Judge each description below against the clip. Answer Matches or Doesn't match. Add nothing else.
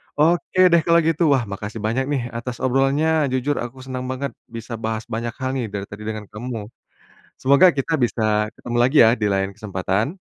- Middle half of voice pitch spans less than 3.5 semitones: Doesn't match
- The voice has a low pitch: Matches